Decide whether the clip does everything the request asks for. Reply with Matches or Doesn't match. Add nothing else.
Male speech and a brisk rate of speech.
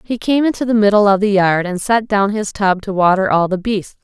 Doesn't match